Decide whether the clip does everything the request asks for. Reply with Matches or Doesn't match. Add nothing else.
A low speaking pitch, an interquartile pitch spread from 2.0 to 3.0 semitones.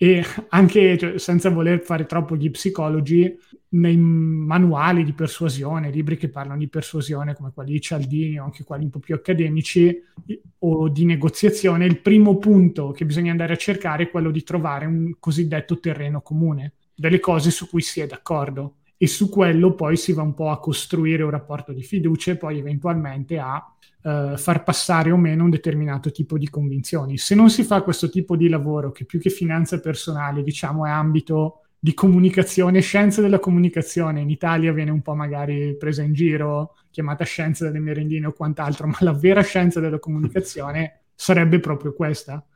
Doesn't match